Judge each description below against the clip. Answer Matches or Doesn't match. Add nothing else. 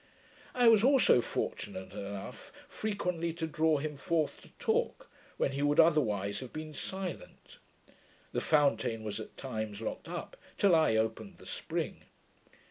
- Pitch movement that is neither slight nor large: Doesn't match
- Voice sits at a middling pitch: Matches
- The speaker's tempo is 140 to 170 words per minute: Matches